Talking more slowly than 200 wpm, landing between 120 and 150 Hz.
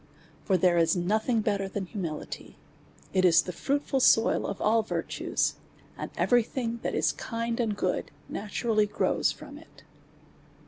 No: average, 150 wpm; high, 210 Hz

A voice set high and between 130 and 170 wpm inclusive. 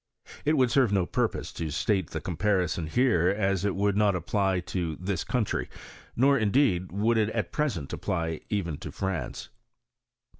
No: very low, 95 Hz; average, 160 wpm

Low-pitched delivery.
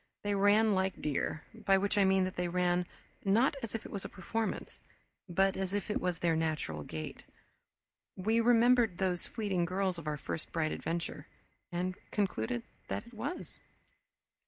No: high, 190 Hz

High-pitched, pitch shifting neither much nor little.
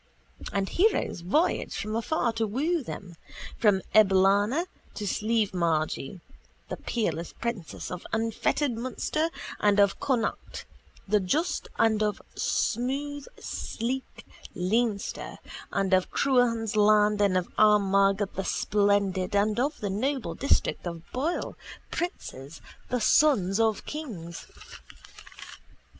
Yes: high, 210 Hz; average, 4.2 semitones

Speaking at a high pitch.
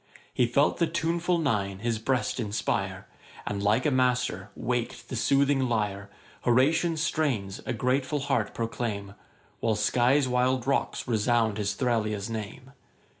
No: low, 120 Hz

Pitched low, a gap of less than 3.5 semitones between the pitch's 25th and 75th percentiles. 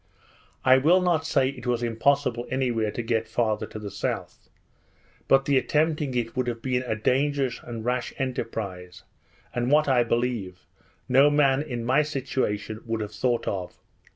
Yes: low, 125 Hz; average, 3.0 semitones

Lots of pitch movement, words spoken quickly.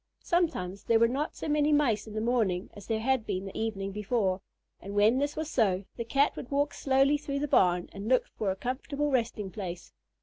Yes: wide, 5.9 semitones; fast, 215 wpm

